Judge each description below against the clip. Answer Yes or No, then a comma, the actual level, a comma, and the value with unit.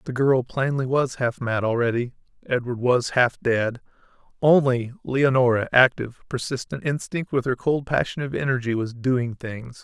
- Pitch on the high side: No, low, 125 Hz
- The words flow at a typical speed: Yes, average, 155 wpm